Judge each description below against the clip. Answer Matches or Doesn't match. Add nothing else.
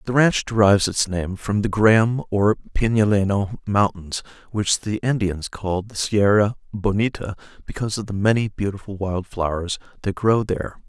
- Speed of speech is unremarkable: Matches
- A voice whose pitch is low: Matches